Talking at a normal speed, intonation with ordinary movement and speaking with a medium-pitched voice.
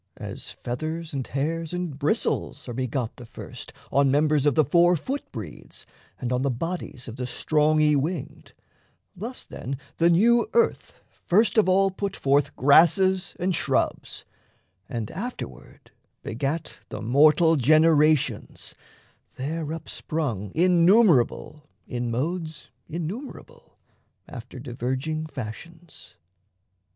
No: slow, 120 wpm; average, 4.7 semitones; medium, 155 Hz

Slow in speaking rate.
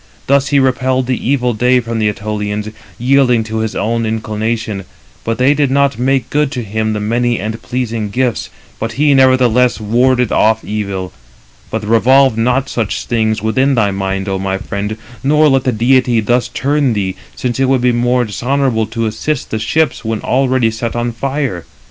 No: average, 185 wpm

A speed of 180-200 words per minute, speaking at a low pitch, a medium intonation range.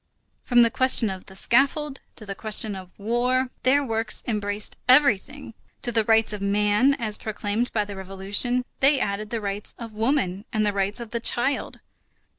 No: average, 185 wpm; high, 220 Hz; average, 3.3 semitones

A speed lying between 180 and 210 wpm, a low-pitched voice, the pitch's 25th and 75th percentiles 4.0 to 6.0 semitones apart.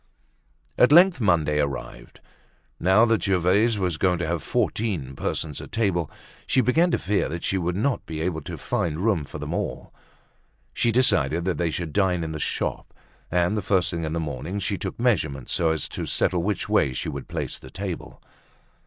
Yes: average, 195 wpm; very low, 90 Hz; average, 4.5 semitones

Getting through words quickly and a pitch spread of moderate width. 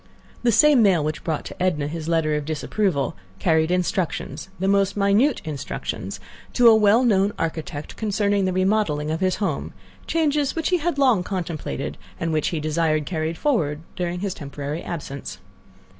No: average, 160 wpm; average, 5.0 semitones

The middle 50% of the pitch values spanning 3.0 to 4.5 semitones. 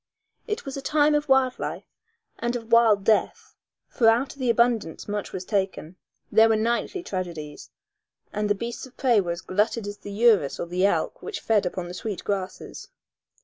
Yes: average, 4.0 semitones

